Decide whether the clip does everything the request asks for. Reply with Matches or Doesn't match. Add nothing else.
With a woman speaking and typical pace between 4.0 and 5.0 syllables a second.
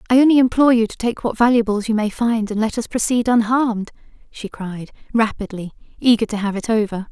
Doesn't match